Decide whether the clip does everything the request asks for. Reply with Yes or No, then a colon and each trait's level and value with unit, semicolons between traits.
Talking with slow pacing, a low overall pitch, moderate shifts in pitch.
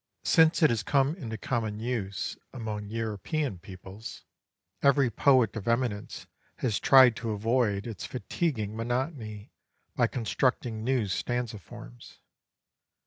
Yes: slow, 120 wpm; low, 115 Hz; average, 3.5 semitones